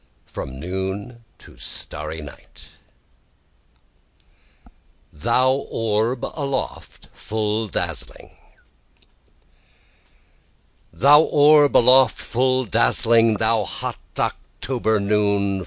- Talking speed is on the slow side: Yes, slow, 75 wpm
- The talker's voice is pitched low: Yes, low, 110 Hz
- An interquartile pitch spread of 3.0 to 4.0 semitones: No, average, 4.4 semitones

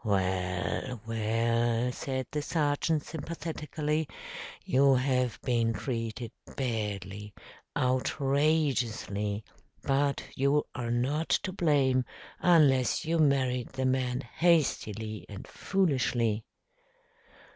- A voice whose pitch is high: No, low, 130 Hz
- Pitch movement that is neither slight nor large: Yes, average, 4.2 semitones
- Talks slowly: Yes, slow, 90 wpm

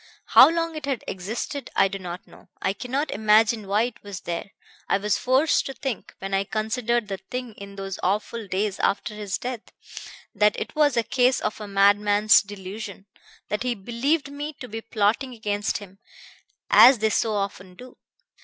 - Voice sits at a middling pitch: No, high, 215 Hz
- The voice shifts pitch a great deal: No, average, 3.9 semitones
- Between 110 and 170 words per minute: No, average, 180 wpm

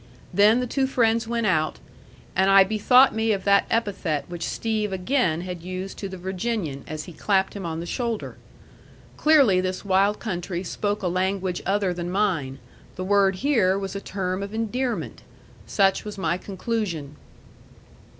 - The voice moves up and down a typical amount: Yes, average, 3.1 semitones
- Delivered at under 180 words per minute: Yes, average, 165 wpm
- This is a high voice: Yes, high, 195 Hz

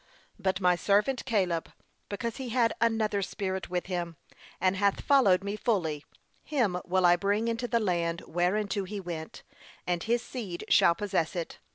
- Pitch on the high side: Yes, high, 195 Hz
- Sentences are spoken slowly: No, average, 165 wpm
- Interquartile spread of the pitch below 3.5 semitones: No, average, 3.8 semitones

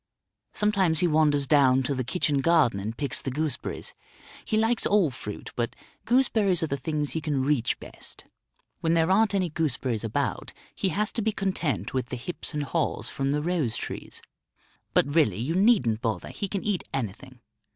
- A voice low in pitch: No, medium, 150 Hz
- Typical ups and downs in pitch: No, wide, 6.2 semitones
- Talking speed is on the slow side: No, average, 180 wpm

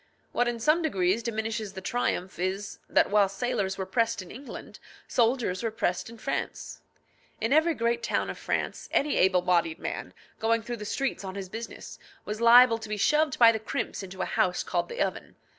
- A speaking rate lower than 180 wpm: No, average, 195 wpm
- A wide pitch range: No, average, 3.9 semitones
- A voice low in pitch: No, high, 225 Hz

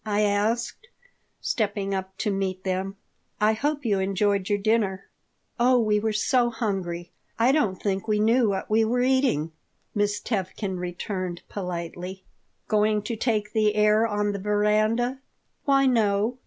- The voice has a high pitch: Yes, high, 210 Hz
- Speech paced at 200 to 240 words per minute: No, average, 150 wpm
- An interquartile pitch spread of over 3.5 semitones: No, average, 2.7 semitones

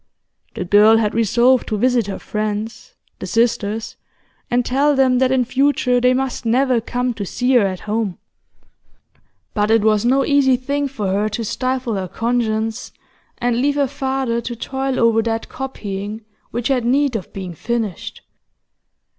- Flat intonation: No, average, 3.2 semitones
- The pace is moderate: Yes, average, 165 wpm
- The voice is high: Yes, high, 235 Hz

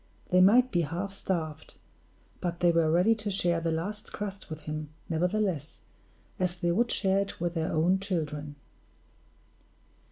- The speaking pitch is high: No, medium, 175 Hz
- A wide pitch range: No, average, 3.4 semitones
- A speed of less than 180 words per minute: Yes, average, 155 wpm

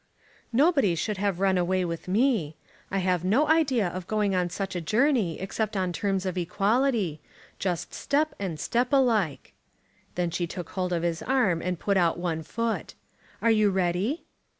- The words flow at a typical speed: Yes, average, 175 wpm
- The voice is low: No, high, 190 Hz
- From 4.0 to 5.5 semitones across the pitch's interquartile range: Yes, average, 4.5 semitones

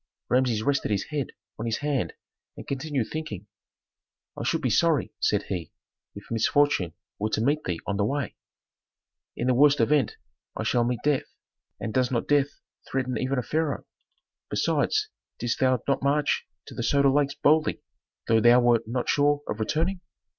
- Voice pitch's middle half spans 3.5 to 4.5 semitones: Yes, average, 4.1 semitones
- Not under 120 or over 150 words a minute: No, average, 170 wpm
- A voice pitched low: Yes, low, 130 Hz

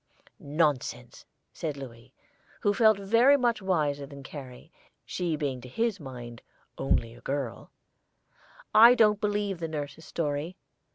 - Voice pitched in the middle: Yes, medium, 155 Hz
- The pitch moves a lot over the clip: Yes, wide, 7.0 semitones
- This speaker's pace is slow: Yes, slow, 125 wpm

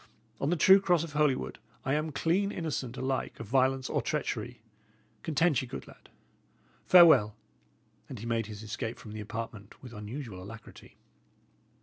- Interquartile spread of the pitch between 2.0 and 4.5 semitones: No, average, 5.3 semitones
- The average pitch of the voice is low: Yes, low, 130 Hz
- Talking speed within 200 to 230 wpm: No, average, 155 wpm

